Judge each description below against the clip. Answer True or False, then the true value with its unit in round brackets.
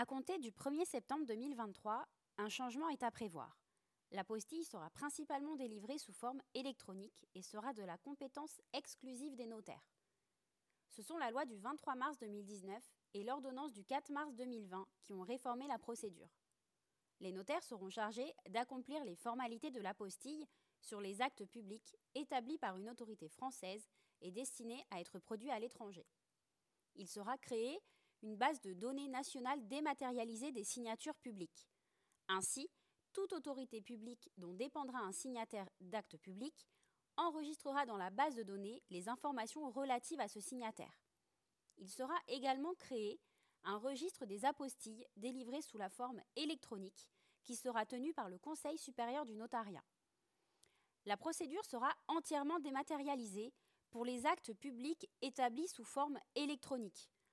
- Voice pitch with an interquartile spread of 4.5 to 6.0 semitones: True (5.0 semitones)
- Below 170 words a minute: True (150 wpm)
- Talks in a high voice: True (250 Hz)